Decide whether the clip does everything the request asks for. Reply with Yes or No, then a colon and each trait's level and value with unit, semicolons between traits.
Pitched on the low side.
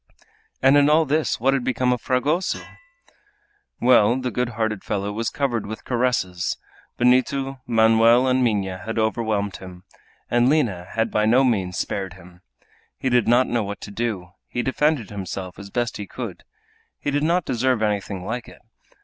Yes: low, 115 Hz